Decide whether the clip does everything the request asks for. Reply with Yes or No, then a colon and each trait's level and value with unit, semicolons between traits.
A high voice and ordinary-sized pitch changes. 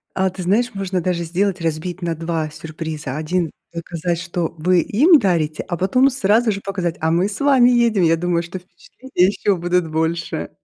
No: medium, 180 Hz; average, 3.1 semitones